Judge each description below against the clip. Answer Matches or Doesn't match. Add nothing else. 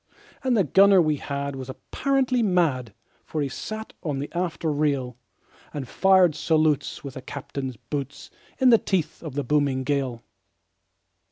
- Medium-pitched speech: Matches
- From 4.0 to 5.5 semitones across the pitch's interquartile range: Matches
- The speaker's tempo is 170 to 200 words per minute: Doesn't match